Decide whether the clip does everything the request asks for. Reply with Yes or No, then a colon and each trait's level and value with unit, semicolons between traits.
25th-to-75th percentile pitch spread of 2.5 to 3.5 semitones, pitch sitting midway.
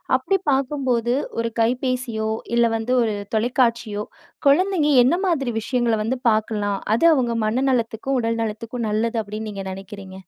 No: average, 2.8 semitones; high, 230 Hz